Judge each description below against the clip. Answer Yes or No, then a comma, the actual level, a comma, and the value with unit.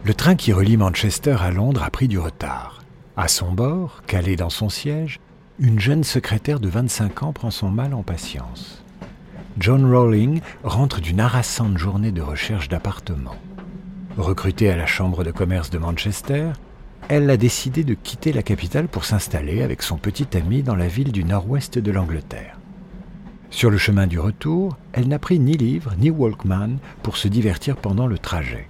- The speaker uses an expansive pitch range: Yes, wide, 6.7 semitones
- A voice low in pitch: Yes, low, 110 Hz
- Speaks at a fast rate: No, average, 175 wpm